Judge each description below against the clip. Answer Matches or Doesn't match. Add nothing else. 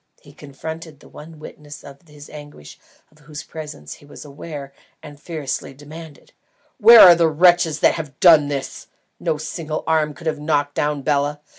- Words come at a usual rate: Matches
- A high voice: Doesn't match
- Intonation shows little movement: Matches